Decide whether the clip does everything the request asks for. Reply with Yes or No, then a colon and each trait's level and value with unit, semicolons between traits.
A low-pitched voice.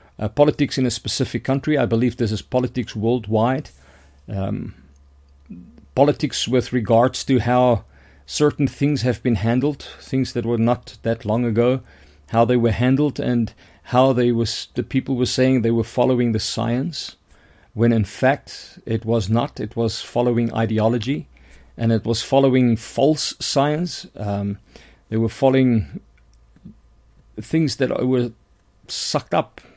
Yes: low, 120 Hz